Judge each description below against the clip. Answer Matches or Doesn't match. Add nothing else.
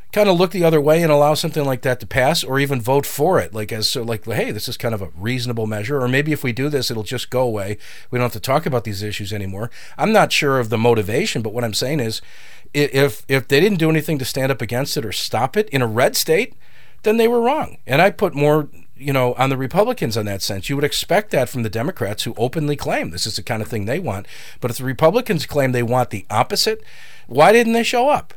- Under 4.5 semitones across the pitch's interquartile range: Doesn't match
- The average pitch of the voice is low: Matches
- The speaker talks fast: Matches